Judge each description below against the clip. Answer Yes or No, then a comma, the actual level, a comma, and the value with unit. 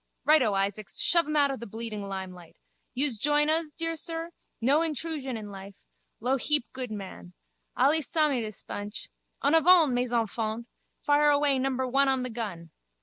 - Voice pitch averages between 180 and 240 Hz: No, very high, 260 Hz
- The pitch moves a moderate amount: No, wide, 5.7 semitones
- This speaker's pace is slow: No, average, 170 wpm